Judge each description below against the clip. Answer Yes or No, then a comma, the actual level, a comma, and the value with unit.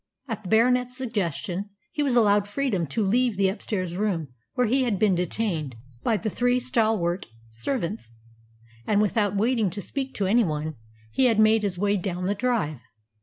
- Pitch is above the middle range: Yes, high, 210 Hz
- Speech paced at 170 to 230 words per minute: Yes, average, 175 wpm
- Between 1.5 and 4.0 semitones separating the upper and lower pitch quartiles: No, average, 4.6 semitones